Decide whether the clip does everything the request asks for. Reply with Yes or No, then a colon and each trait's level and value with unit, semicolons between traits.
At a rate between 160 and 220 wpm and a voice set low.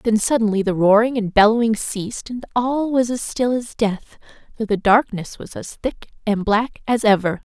No: average, 190 wpm; high, 220 Hz